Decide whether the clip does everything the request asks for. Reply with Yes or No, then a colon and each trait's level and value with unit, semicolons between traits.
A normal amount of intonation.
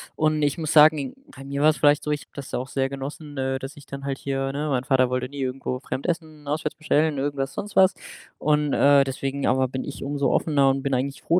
No: narrow, 1.9 semitones